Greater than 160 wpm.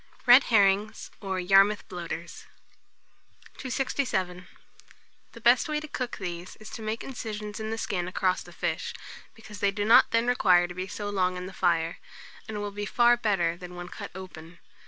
Yes: average, 175 wpm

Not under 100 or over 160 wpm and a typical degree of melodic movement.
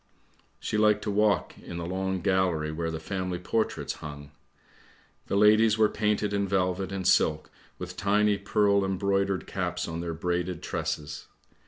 Yes: average, 155 wpm; average, 3.1 semitones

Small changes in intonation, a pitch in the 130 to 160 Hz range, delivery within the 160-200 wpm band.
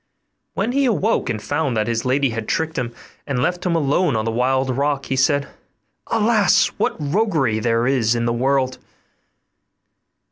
No: average, 5.3 semitones; low, 135 Hz; average, 170 wpm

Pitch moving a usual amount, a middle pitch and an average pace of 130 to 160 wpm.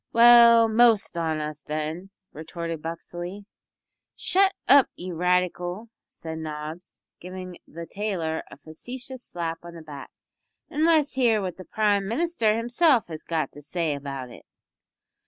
No: wide, 6.3 semitones; medium, 180 Hz; average, 145 wpm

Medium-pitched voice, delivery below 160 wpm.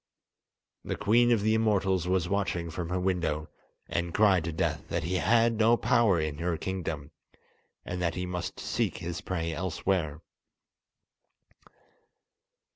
No: very low, 90 Hz; average, 140 wpm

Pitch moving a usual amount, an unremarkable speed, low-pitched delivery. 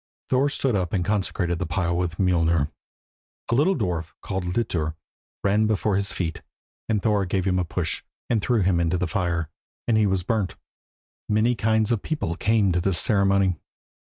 Yes: average, 3.7 semitones; average, 180 wpm; very low, 95 Hz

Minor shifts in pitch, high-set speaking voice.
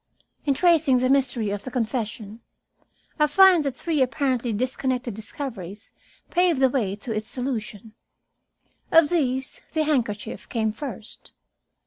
No: average, 4.5 semitones; very high, 255 Hz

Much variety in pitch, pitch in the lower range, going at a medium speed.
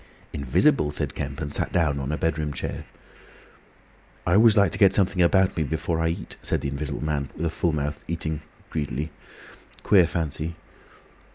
No: average, 3.0 semitones; very low, 80 Hz; average, 175 wpm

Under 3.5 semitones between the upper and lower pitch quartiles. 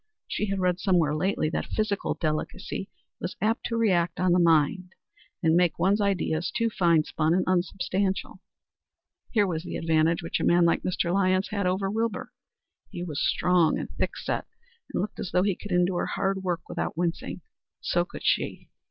Yes: narrow, 2.5 semitones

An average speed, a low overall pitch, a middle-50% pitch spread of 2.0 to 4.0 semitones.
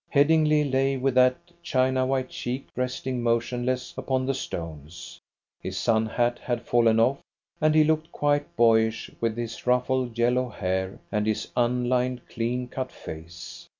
Yes: average, 150 wpm; low, 125 Hz; narrow, 2.4 semitones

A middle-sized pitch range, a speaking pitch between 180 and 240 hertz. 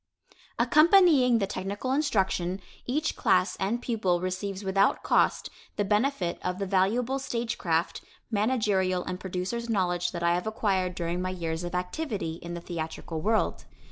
Yes: average, 4.4 semitones; high, 190 Hz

